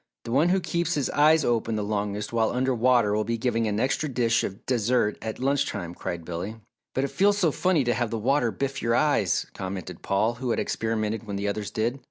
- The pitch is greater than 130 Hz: No, low, 115 Hz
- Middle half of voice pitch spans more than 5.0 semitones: No, average, 4.4 semitones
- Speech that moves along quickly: Yes, fast, 230 wpm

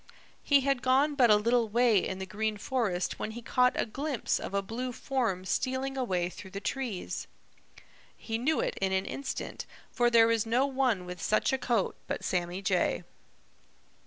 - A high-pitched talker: Yes, high, 230 Hz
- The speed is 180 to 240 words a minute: Yes, average, 185 wpm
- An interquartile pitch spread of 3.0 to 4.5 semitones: No, average, 4.9 semitones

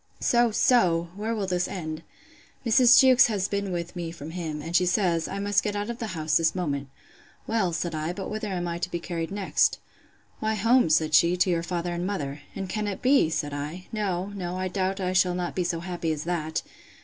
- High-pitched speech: No, medium, 180 Hz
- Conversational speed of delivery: No, fast, 220 wpm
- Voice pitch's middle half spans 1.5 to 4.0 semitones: Yes, average, 3.4 semitones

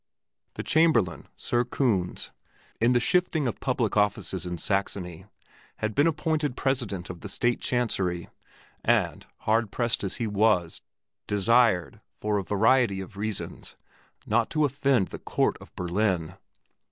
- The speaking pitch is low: Yes, low, 110 Hz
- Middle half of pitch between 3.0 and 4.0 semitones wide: No, average, 4.6 semitones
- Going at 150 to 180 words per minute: No, average, 140 wpm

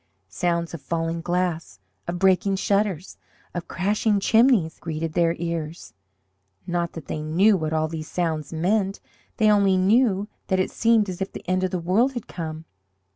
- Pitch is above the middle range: No, medium, 180 Hz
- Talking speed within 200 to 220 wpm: No, average, 170 wpm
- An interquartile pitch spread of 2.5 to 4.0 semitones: Yes, average, 3.3 semitones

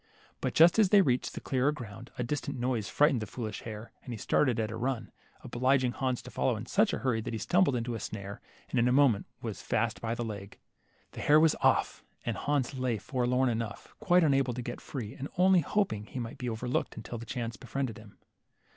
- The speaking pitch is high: No, low, 125 Hz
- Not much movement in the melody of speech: No, average, 3.4 semitones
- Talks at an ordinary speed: No, fast, 225 wpm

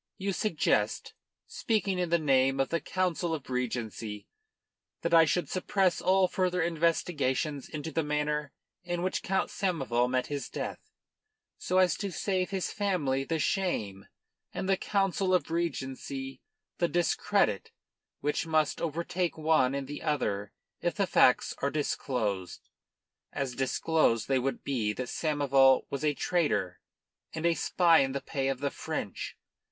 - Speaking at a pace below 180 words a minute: Yes, average, 150 wpm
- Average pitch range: Yes, average, 4.8 semitones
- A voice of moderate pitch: Yes, medium, 150 Hz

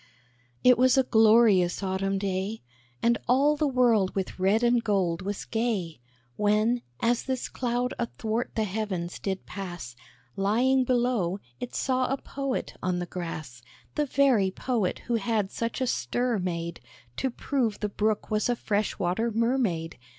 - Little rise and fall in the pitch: No, average, 4.4 semitones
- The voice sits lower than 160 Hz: No, high, 220 Hz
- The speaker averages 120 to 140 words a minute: No, average, 155 wpm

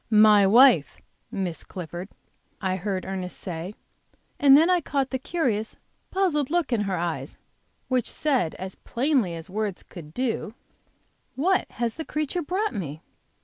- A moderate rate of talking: Yes, average, 145 wpm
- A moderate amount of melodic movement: No, wide, 7.3 semitones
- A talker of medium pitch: No, high, 220 Hz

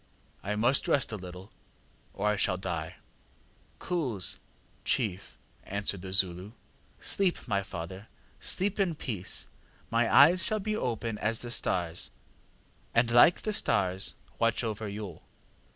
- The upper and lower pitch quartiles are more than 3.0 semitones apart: Yes, average, 4.8 semitones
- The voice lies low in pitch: Yes, low, 105 Hz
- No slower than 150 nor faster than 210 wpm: No, slow, 135 wpm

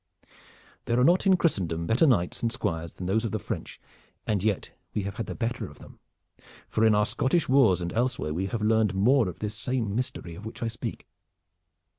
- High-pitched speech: No, low, 110 Hz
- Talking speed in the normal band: No, fast, 210 wpm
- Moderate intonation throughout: Yes, average, 4.1 semitones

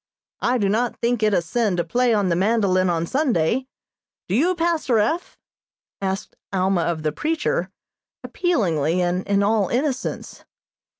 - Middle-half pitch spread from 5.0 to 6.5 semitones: Yes, wide, 5.6 semitones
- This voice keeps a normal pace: Yes, average, 155 wpm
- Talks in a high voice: Yes, high, 205 Hz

